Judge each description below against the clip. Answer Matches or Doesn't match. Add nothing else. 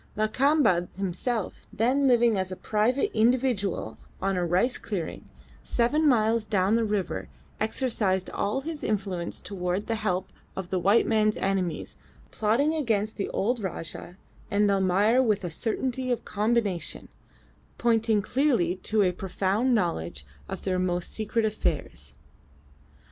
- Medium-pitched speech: Doesn't match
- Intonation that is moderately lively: Matches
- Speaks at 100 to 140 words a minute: Matches